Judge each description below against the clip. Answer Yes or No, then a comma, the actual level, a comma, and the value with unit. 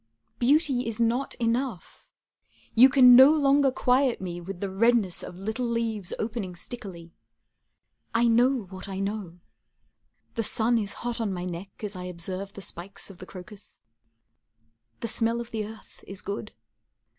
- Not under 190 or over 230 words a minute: No, average, 155 wpm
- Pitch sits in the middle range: No, high, 220 Hz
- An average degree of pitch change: Yes, average, 4.2 semitones